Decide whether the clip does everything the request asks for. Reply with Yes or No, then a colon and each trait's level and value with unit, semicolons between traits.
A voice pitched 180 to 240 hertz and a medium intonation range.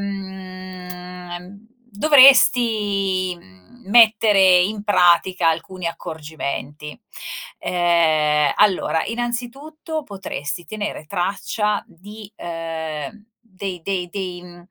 Yes: medium, 185 Hz; average, 3.4 semitones